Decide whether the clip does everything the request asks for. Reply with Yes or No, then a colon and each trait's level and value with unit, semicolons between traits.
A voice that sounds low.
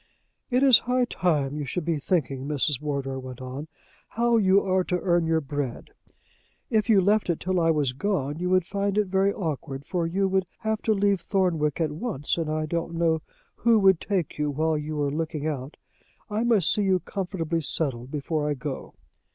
No: medium, 165 Hz